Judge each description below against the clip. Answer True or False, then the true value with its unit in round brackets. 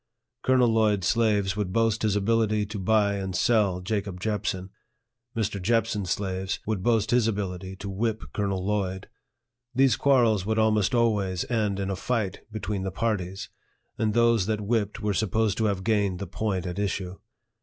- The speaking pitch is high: False (105 Hz)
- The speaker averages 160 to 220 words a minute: True (165 wpm)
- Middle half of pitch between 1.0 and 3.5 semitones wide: True (2.6 semitones)